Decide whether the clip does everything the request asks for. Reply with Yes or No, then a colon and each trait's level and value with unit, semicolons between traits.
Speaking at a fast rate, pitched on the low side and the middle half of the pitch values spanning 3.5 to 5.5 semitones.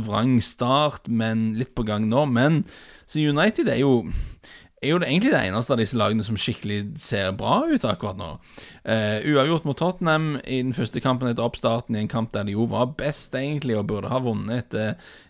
Yes: fast, 210 wpm; low, 120 Hz; average, 3.9 semitones